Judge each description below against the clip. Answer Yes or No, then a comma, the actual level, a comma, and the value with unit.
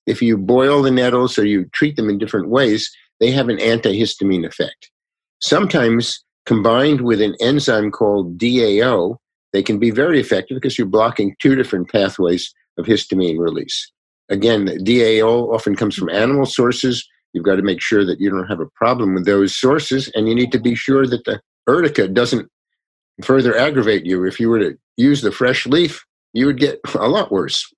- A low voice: Yes, low, 115 Hz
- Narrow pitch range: No, average, 4.2 semitones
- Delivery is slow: No, average, 190 wpm